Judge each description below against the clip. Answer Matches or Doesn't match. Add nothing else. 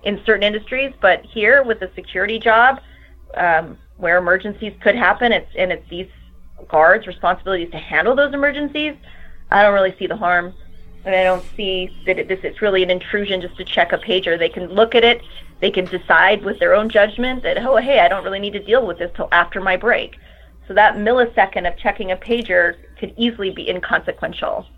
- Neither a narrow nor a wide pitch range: Matches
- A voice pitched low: Doesn't match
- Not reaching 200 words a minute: Doesn't match